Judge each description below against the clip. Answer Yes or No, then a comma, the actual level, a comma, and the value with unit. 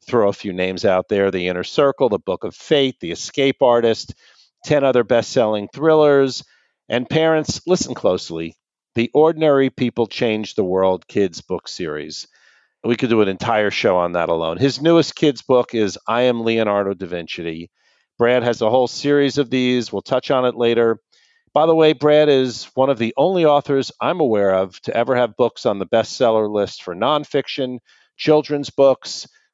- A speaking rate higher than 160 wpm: Yes, average, 185 wpm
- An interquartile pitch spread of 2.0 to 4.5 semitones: No, wide, 5.6 semitones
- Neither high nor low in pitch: No, low, 125 Hz